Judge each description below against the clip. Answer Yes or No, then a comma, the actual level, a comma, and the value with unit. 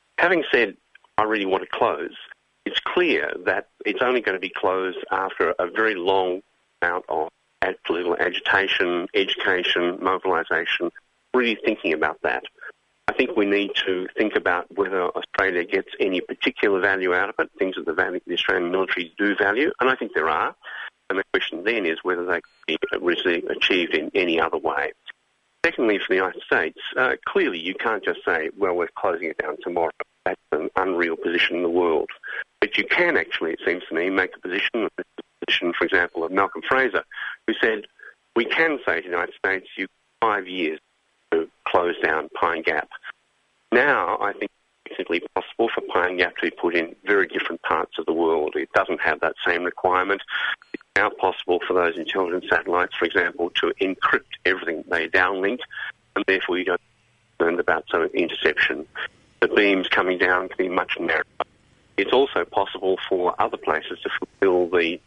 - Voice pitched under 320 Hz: No, very high, 390 Hz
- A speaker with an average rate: Yes, average, 180 wpm